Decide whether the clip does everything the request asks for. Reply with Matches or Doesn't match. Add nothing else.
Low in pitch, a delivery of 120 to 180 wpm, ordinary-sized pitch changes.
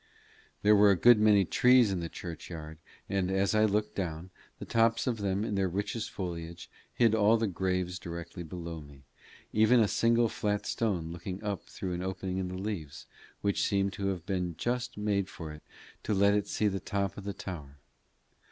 Doesn't match